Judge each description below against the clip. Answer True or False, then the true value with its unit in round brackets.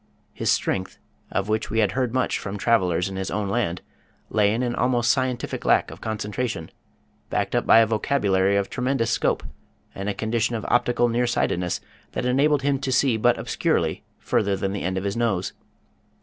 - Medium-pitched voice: False (110 Hz)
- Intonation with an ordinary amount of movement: True (3.9 semitones)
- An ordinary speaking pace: True (190 wpm)